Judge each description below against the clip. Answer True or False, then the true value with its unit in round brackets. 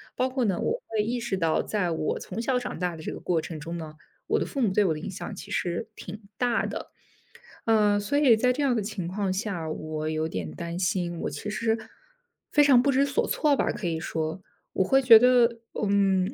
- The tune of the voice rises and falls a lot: True (6.0 semitones)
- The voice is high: True (200 Hz)